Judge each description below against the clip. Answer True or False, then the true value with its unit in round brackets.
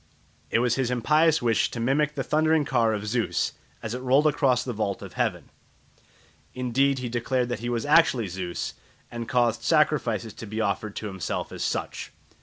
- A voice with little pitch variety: False (3.2 semitones)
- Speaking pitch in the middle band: False (120 Hz)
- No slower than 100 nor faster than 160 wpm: False (185 wpm)